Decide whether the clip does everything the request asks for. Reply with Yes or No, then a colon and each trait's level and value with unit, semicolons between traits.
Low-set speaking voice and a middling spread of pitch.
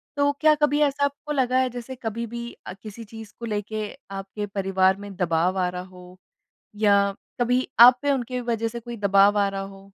No: high, 215 Hz; average, 4.0 semitones